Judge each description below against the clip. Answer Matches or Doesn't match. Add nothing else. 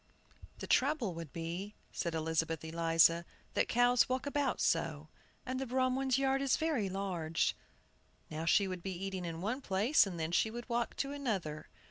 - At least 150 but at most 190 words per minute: Matches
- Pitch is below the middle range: Doesn't match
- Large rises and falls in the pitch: Matches